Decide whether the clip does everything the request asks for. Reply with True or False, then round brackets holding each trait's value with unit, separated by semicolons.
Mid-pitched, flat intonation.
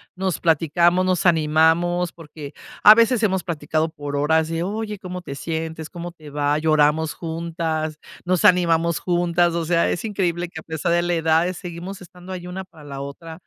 True (170 Hz; 2.0 semitones)